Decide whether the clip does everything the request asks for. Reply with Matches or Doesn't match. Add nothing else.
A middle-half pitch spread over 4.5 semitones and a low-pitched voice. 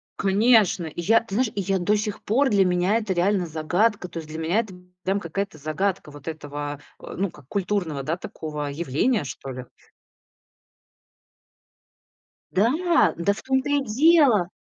Doesn't match